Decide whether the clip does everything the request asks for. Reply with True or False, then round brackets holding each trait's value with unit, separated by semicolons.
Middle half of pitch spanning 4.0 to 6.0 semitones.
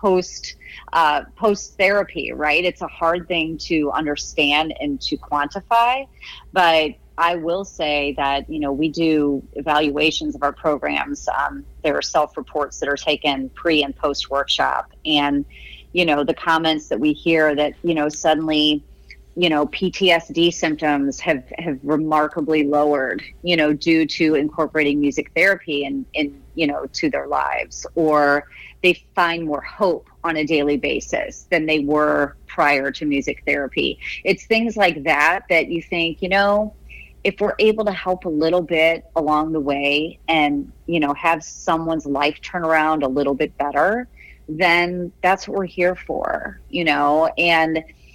False (3.0 semitones)